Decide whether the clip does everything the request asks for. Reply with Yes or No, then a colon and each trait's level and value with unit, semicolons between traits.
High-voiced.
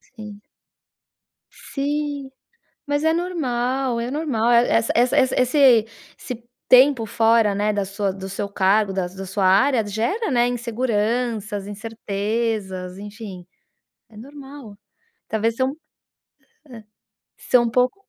Yes: high, 230 Hz